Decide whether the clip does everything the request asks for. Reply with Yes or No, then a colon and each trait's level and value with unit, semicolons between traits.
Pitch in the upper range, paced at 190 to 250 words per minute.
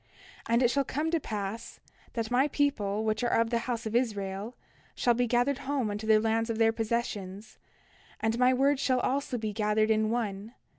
Yes: high, 230 Hz; average, 200 wpm